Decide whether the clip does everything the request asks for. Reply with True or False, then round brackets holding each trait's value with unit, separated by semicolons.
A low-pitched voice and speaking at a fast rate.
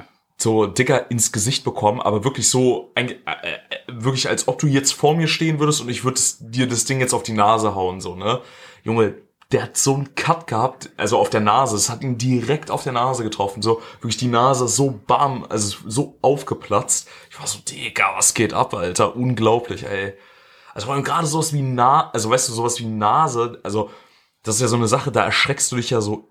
True (120 Hz; 210 wpm)